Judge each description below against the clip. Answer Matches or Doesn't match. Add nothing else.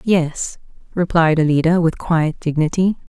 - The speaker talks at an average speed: Doesn't match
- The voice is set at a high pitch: Doesn't match